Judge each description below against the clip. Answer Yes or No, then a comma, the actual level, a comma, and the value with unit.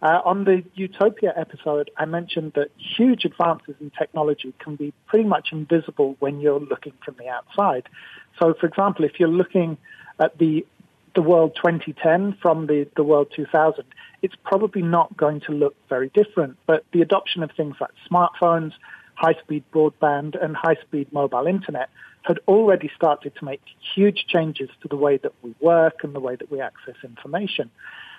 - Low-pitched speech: No, medium, 160 Hz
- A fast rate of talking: No, average, 190 wpm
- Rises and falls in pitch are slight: No, average, 3.1 semitones